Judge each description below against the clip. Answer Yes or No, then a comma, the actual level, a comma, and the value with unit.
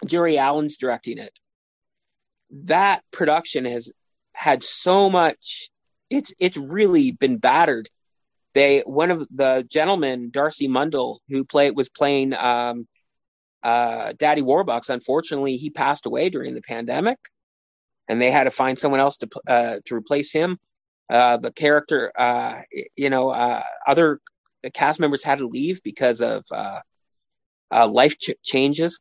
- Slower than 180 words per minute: Yes, average, 145 wpm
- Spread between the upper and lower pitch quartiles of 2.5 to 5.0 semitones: Yes, average, 4.0 semitones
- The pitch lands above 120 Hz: Yes, medium, 140 Hz